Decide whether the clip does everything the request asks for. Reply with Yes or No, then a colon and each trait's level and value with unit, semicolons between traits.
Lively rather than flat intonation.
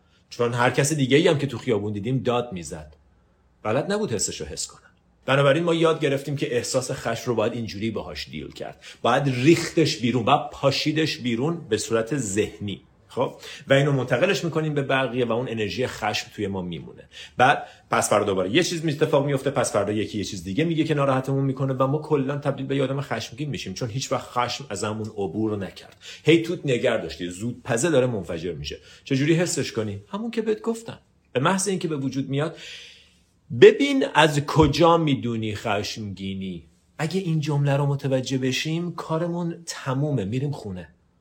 Yes: wide, 6.0 semitones